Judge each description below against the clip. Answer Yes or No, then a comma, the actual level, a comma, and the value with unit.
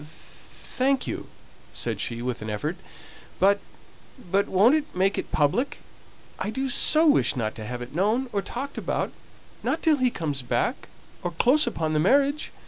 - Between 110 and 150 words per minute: No, average, 170 wpm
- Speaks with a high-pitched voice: Yes, high, 200 Hz